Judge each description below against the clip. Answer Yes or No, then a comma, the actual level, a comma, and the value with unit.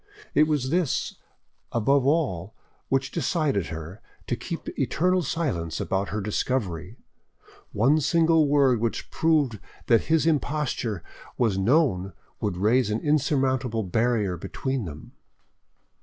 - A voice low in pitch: Yes, low, 125 Hz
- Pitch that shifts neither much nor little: No, wide, 6.9 semitones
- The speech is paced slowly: Yes, slow, 120 wpm